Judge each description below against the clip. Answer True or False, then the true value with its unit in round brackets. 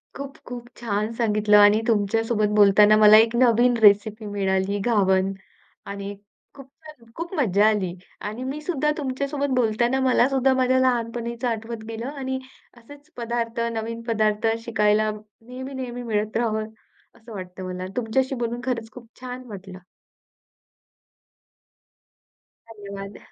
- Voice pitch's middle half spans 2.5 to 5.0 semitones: True (3.1 semitones)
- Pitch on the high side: True (230 Hz)